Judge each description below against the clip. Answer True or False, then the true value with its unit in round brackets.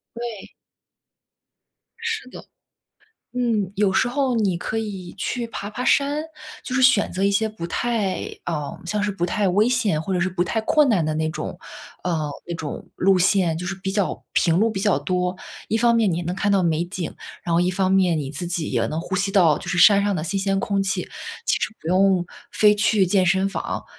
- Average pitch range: True (3.4 semitones)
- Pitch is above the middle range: True (195 Hz)